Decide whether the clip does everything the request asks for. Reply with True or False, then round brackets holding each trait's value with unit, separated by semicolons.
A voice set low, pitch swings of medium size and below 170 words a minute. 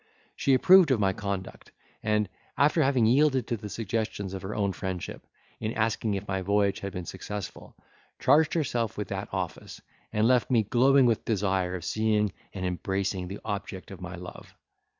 False (105 Hz; 3.7 semitones; 175 wpm)